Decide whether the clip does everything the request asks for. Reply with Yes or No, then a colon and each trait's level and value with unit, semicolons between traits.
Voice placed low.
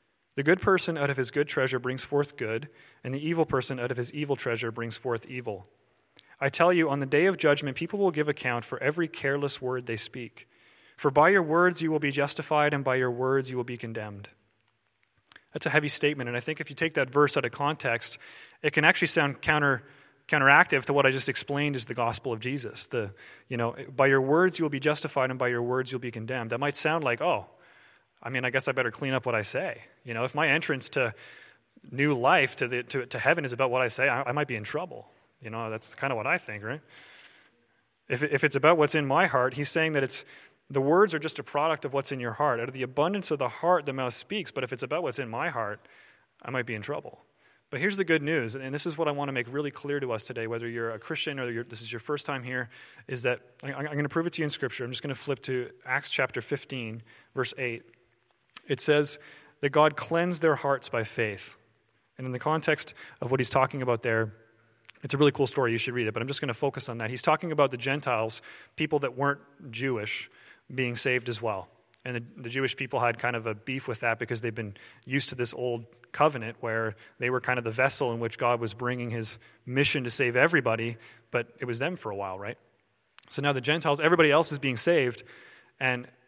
Yes: low, 130 Hz